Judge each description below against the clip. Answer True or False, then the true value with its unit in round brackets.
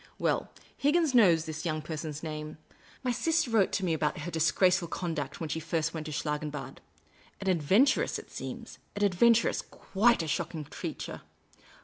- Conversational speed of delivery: True (165 wpm)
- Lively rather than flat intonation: False (4.8 semitones)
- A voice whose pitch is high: False (165 Hz)